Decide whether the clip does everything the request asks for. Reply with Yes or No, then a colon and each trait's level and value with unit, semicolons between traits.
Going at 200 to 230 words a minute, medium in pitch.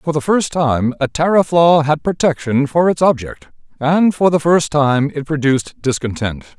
No: average, 180 wpm; medium, 150 Hz